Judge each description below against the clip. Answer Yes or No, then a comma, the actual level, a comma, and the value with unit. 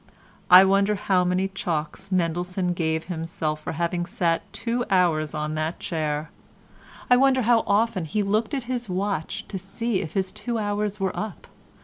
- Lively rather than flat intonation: No, average, 4.1 semitones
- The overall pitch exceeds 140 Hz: Yes, high, 190 Hz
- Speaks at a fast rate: No, average, 165 wpm